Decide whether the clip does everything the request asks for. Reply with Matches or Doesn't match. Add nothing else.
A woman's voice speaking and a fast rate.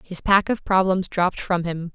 Matches